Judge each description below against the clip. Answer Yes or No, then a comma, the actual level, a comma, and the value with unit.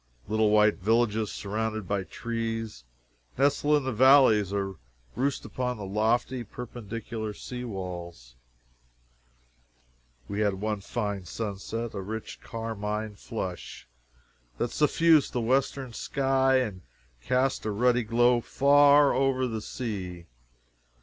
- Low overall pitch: Yes, low, 110 Hz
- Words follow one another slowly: Yes, slow, 115 wpm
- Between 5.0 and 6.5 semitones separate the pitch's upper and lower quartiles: No, average, 3.6 semitones